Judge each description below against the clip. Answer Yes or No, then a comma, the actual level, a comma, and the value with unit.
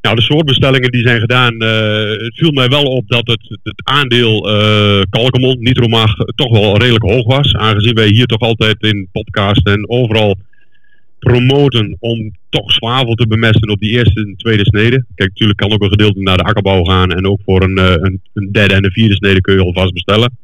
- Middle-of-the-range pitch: No, low, 110 Hz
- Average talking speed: No, fast, 210 wpm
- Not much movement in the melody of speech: No, average, 3.1 semitones